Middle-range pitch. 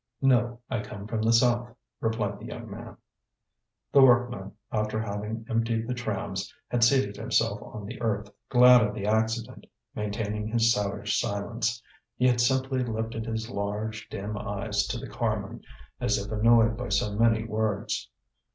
No: low, 110 Hz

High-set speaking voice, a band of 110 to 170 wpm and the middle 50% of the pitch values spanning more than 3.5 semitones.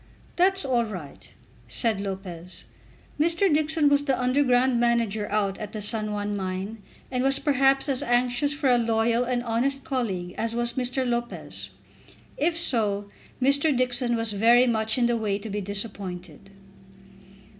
Yes: high, 235 Hz; average, 155 wpm; average, 4.3 semitones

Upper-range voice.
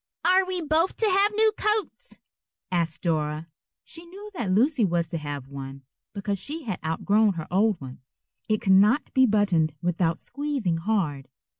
Yes: high, 200 Hz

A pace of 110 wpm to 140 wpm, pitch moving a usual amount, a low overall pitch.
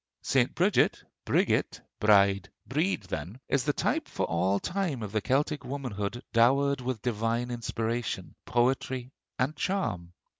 Yes: slow, 135 wpm; average, 4.5 semitones; low, 120 Hz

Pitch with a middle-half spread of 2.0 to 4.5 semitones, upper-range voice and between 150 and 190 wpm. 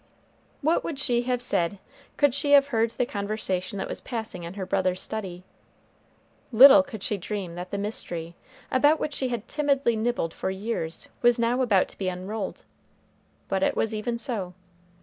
No: average, 4.9 semitones; high, 220 Hz; average, 175 wpm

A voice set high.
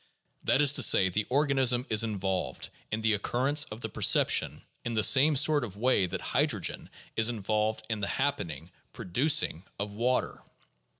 No: low, 115 Hz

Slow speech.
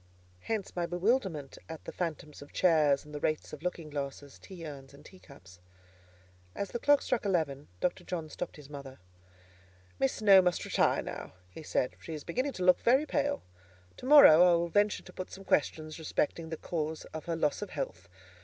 No: average, 190 wpm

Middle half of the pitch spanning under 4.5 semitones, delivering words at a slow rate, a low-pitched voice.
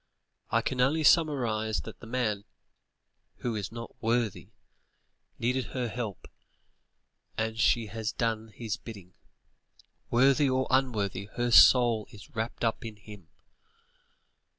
Yes: average, 2.7 semitones; slow, 125 wpm; low, 115 Hz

